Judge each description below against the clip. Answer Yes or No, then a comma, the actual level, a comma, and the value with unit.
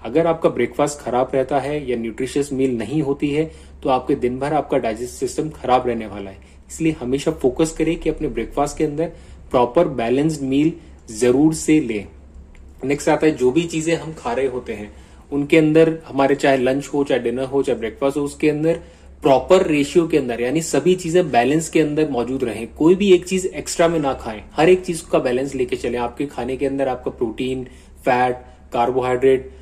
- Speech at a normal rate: No, fast, 200 wpm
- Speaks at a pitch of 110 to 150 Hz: Yes, medium, 140 Hz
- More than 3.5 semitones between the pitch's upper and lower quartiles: Yes, average, 4.1 semitones